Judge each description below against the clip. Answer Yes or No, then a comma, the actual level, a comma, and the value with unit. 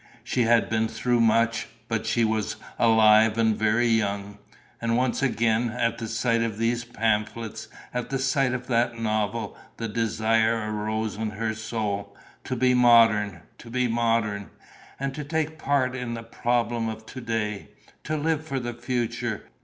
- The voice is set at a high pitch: No, low, 115 Hz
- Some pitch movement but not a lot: No, narrow, 1.8 semitones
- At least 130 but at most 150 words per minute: No, average, 165 wpm